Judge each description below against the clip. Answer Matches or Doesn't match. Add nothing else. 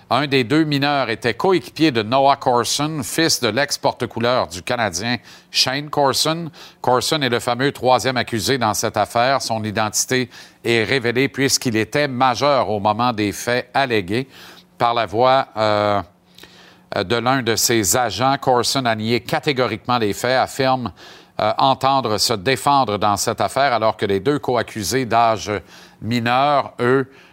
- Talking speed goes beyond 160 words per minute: Doesn't match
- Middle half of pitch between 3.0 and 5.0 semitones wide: Matches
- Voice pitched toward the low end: Matches